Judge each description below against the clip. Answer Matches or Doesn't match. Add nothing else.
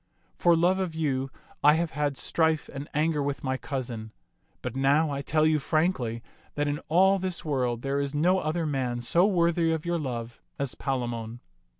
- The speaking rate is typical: Matches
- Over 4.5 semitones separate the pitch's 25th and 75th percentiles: Doesn't match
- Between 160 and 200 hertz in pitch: Doesn't match